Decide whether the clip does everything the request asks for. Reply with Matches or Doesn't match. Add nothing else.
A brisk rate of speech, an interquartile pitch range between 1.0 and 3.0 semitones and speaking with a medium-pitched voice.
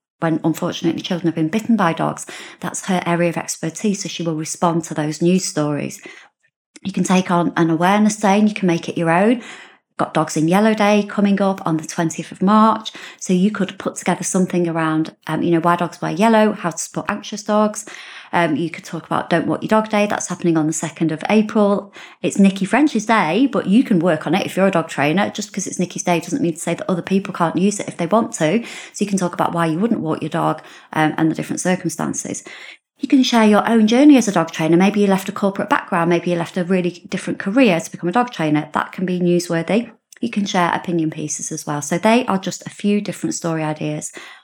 Doesn't match